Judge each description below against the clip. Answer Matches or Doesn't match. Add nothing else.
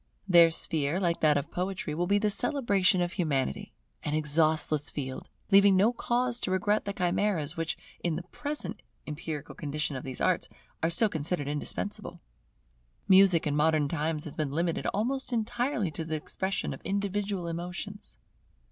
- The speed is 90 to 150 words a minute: Doesn't match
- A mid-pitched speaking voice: Matches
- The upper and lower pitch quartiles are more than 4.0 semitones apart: Matches